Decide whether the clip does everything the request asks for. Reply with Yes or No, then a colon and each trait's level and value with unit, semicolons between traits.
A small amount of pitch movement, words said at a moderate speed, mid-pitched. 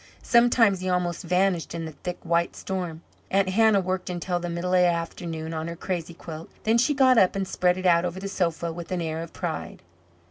No: narrow, 2.1 semitones; fast, 220 wpm; medium, 180 Hz